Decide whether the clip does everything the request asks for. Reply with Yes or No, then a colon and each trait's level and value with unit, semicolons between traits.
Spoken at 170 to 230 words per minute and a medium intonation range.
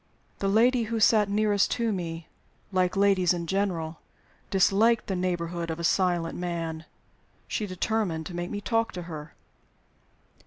No: average, 150 wpm; average, 3.6 semitones